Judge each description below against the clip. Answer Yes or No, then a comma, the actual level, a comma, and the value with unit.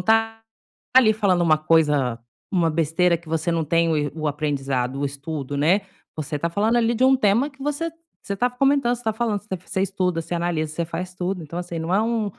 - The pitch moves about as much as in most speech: No, wide, 6.0 semitones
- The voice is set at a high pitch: No, medium, 175 Hz